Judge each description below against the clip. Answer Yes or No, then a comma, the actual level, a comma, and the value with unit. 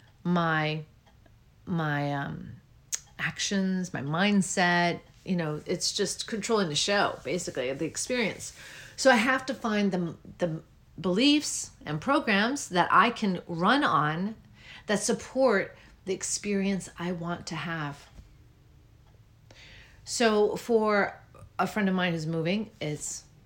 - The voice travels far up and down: Yes, wide, 6.0 semitones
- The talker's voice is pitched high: No, medium, 175 Hz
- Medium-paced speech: No, slow, 125 wpm